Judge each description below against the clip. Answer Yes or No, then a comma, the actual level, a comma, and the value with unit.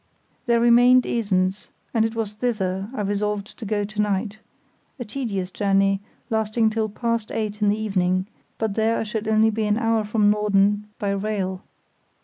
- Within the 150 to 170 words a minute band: Yes, average, 165 wpm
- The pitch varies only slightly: Yes, narrow, 1.9 semitones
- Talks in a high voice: Yes, high, 210 Hz